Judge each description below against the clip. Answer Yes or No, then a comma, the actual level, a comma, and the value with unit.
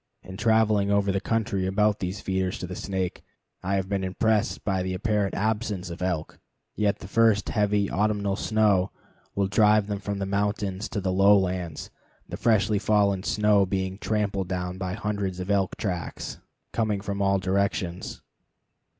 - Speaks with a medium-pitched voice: No, low, 100 Hz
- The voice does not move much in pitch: Yes, narrow, 1.9 semitones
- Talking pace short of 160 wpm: No, average, 165 wpm